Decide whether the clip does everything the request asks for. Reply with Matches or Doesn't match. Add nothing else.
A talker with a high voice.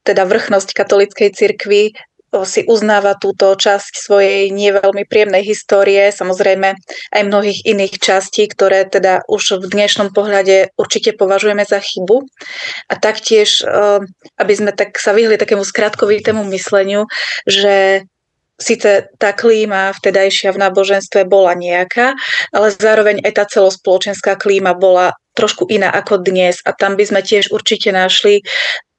Matches